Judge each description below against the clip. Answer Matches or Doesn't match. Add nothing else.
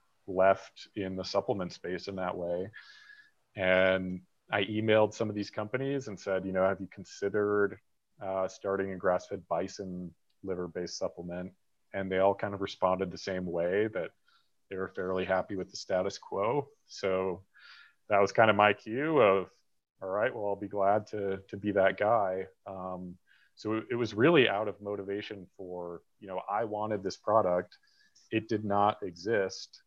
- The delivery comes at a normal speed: Matches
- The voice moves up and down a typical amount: Doesn't match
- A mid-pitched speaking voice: Doesn't match